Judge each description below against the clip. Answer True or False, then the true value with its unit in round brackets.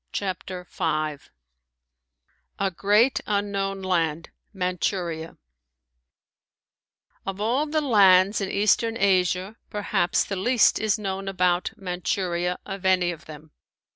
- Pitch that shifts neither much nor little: False (2.3 semitones)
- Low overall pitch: False (190 Hz)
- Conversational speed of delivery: False (105 wpm)